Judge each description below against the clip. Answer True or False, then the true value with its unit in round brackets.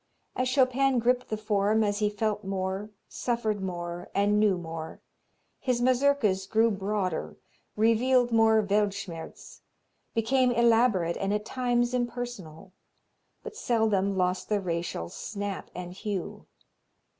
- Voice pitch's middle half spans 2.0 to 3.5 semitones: False (3.9 semitones)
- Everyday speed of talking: False (120 wpm)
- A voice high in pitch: True (210 Hz)